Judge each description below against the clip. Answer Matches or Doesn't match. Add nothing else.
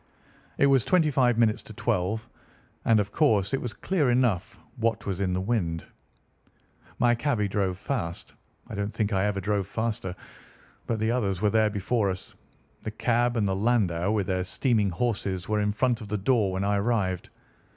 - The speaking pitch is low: Matches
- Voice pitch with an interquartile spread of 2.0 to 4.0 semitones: Matches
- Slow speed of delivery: Doesn't match